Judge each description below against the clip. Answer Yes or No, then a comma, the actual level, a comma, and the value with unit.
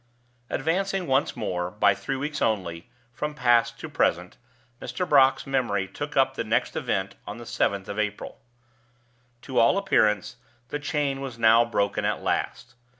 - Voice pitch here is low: Yes, low, 120 Hz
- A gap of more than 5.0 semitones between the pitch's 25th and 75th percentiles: Yes, wide, 5.5 semitones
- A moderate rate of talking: Yes, average, 155 wpm